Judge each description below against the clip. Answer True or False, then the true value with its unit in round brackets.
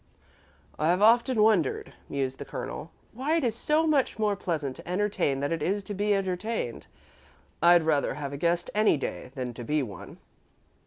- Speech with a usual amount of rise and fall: False (7.0 semitones)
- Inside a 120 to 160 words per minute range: False (175 wpm)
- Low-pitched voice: False (175 Hz)